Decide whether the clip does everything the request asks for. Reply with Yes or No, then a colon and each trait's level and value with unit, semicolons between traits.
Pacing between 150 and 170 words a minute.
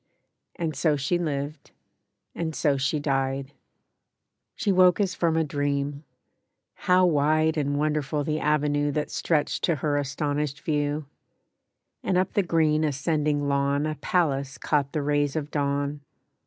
No: average, 140 wpm